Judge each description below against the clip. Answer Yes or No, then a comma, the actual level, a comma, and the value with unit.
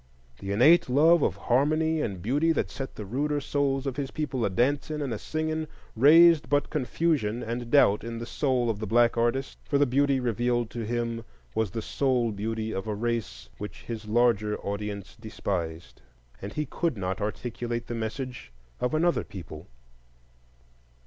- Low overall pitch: Yes, low, 120 Hz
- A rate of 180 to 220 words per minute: No, average, 170 wpm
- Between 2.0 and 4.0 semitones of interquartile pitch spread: No, average, 4.8 semitones